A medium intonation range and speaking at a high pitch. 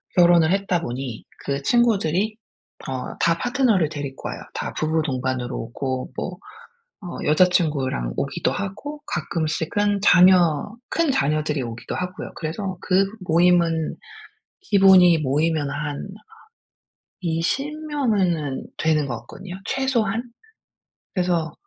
No: average, 4.8 semitones; medium, 170 Hz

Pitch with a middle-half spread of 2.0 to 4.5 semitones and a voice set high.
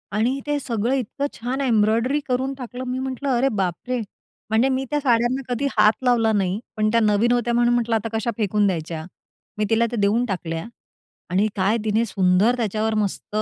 Yes: average, 3.1 semitones; high, 230 Hz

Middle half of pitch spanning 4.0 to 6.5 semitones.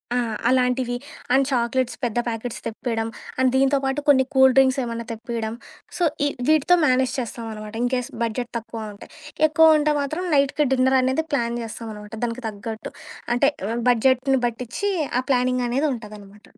No: narrow, 2.6 semitones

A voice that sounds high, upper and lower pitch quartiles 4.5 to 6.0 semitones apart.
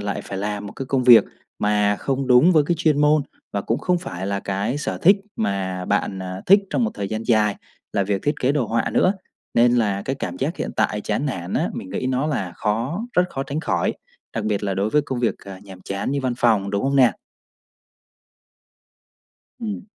No: low, 115 Hz; wide, 5.6 semitones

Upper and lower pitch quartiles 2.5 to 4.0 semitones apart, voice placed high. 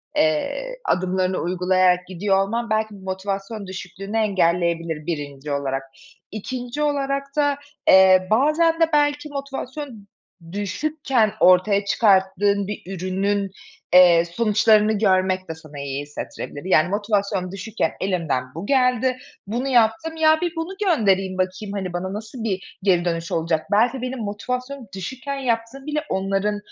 No: wide, 5.4 semitones; high, 200 Hz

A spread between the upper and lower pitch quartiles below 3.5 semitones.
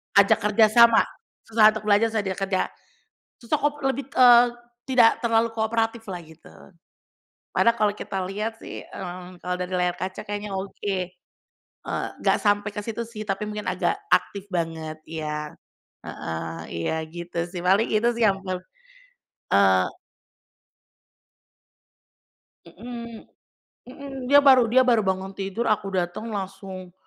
No: average, 3.9 semitones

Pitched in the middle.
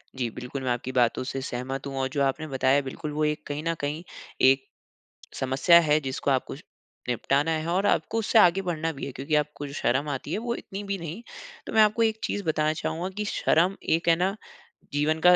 Yes: medium, 150 Hz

